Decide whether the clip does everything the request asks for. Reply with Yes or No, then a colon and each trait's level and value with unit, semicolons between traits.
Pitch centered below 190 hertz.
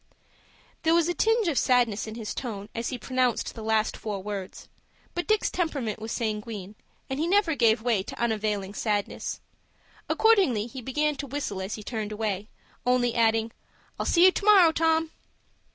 No: high, 235 Hz